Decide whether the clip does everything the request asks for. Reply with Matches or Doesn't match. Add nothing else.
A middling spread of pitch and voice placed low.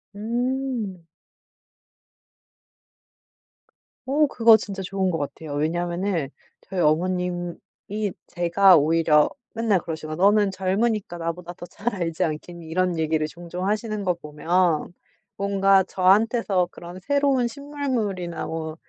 Doesn't match